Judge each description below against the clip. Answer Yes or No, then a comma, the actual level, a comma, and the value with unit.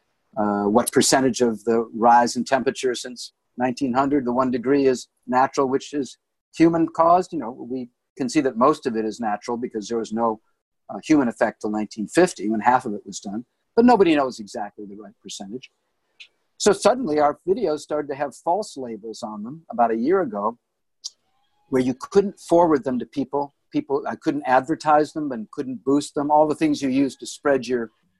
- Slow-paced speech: No, average, 195 wpm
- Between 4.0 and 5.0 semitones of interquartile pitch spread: Yes, average, 4.4 semitones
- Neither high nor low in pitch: No, low, 130 Hz